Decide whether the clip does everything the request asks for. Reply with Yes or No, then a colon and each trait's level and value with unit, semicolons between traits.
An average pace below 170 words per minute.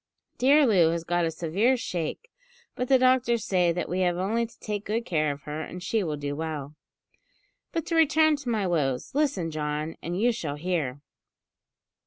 No: average, 190 wpm